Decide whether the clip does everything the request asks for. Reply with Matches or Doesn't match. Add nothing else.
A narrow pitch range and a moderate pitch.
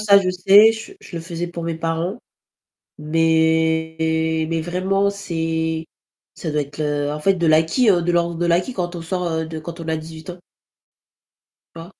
Matches